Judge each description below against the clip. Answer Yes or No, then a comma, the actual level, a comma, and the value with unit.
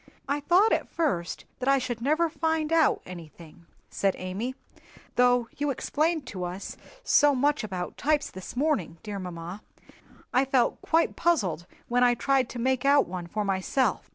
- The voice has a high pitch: Yes, very high, 250 Hz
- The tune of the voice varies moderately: No, wide, 7.6 semitones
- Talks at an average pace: Yes, average, 165 wpm